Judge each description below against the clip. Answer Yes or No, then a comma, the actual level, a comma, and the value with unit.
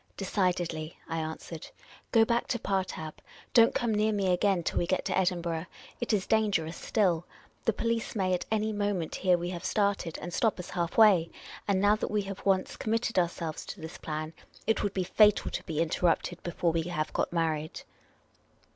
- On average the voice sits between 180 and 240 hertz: Yes, medium, 185 Hz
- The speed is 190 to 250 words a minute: Yes, average, 200 wpm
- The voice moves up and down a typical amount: Yes, average, 3.8 semitones